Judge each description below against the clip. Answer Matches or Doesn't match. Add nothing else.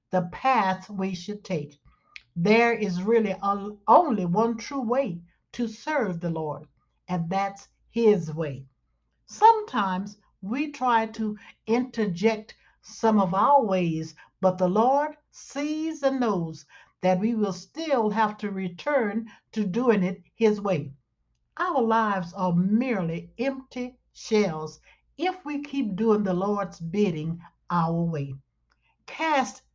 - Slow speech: Matches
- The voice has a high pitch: Matches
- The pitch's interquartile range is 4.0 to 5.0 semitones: Matches